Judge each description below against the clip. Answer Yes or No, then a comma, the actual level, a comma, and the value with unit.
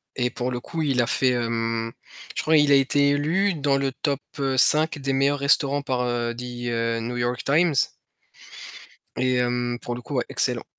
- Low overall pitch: Yes, low, 130 Hz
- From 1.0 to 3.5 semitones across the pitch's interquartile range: Yes, average, 2.8 semitones